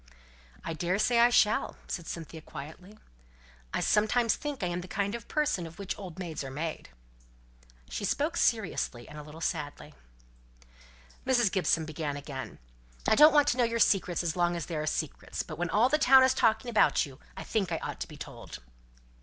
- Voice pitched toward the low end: No, medium, 185 Hz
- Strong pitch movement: Yes, wide, 6.4 semitones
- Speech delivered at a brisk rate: No, average, 190 wpm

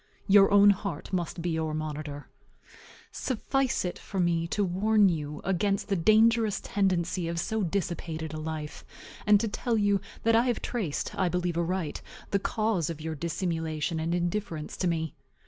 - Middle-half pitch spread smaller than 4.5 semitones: Yes, average, 4.1 semitones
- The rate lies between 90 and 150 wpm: No, average, 165 wpm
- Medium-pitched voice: Yes, medium, 180 Hz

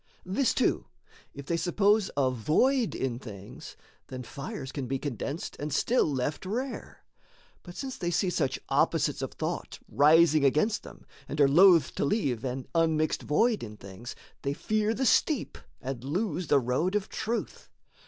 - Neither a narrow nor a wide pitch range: No, wide, 7.2 semitones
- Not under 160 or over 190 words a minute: Yes, average, 165 wpm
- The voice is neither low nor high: Yes, medium, 155 Hz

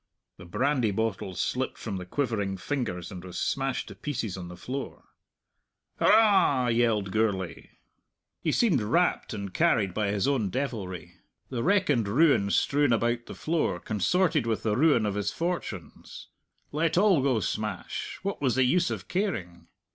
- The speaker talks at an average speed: Yes, average, 160 wpm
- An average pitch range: No, wide, 6.5 semitones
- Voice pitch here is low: Yes, low, 115 Hz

